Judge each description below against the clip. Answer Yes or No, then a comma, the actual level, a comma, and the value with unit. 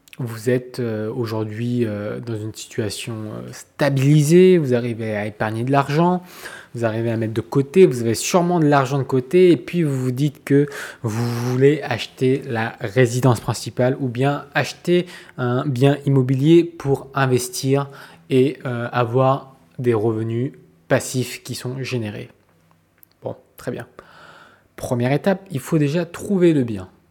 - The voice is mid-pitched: No, low, 130 Hz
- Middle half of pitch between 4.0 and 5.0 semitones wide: No, average, 3.5 semitones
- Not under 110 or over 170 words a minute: Yes, slow, 145 wpm